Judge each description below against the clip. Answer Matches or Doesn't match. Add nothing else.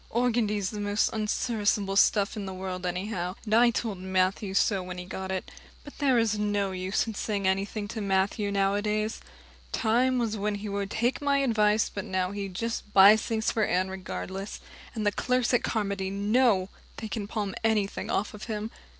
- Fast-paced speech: Doesn't match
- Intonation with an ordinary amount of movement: Doesn't match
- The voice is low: Doesn't match